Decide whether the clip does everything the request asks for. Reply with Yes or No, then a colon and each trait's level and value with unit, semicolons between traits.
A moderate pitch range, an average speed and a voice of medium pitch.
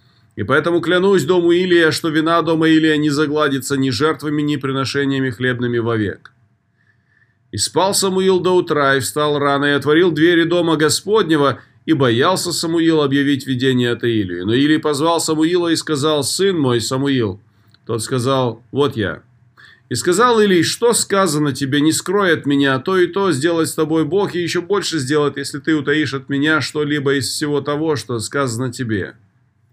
No: average, 4.1 semitones; fast, 170 wpm; medium, 150 Hz